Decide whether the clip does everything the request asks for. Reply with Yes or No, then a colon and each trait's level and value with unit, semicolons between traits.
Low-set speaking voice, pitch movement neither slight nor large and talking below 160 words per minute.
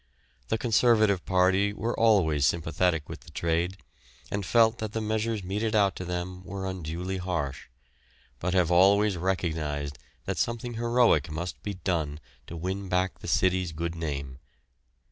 Yes: very low, 90 Hz; average, 3.8 semitones; average, 150 wpm